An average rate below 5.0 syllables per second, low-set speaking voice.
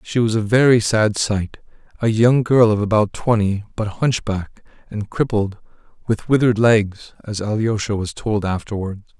Yes: 4.6 syllables/s; low, 110 Hz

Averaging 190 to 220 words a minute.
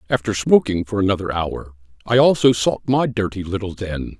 No: average, 170 wpm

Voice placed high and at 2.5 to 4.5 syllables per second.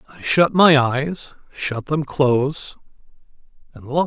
No: medium, 145 Hz; 3.9 syllables/s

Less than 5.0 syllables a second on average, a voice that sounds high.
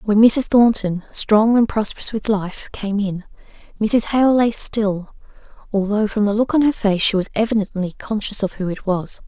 Yes: 4.7 syllables/s; high, 210 Hz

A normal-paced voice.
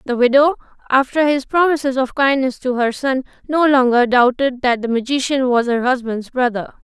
Yes: average, 175 wpm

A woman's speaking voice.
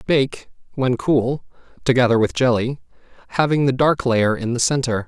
No: male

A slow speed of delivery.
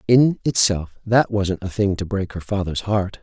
No: fast, 205 wpm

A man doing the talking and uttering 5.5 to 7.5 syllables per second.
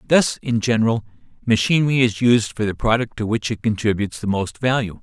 Yes: male; 5.9 syllables/s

